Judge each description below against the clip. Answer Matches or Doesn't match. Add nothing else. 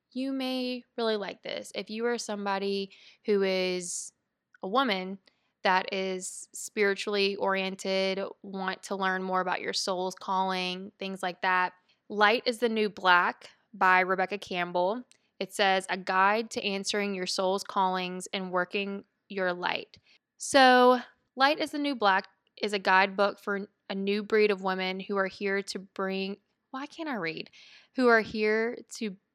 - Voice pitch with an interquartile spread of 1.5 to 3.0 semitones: Matches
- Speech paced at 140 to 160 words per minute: Matches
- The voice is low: Doesn't match